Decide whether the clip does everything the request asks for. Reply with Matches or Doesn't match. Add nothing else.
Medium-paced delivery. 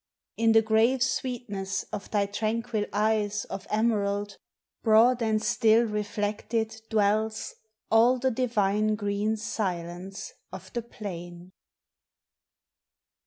Doesn't match